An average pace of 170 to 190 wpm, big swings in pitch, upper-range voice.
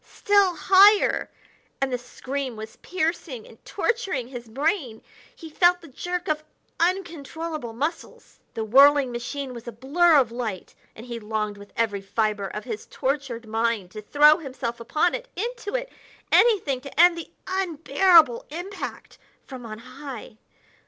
No: average, 150 wpm; wide, 6.8 semitones; very high, 275 Hz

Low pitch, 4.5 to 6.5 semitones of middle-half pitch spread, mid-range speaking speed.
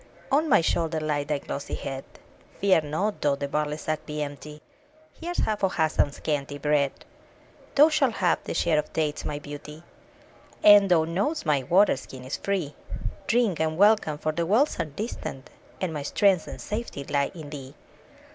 No: medium, 155 Hz; average, 5.3 semitones; average, 175 wpm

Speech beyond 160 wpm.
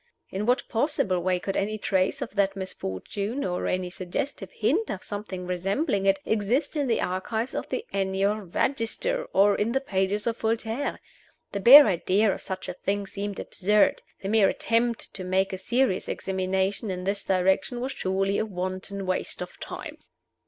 Yes: average, 175 wpm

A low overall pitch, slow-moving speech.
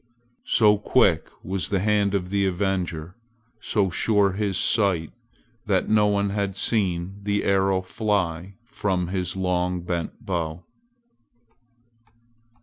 Yes: very low, 95 Hz; slow, 120 wpm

